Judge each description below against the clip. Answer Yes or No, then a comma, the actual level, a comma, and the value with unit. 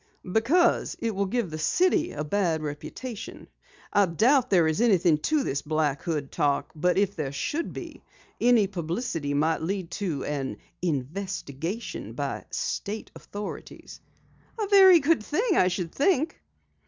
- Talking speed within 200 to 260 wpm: No, average, 145 wpm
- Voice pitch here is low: No, high, 190 Hz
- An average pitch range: No, wide, 7.5 semitones